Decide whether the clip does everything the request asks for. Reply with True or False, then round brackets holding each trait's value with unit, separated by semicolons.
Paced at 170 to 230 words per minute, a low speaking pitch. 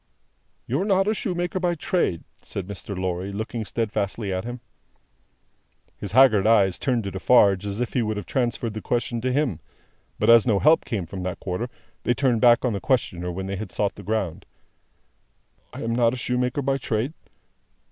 True (190 wpm; 115 Hz)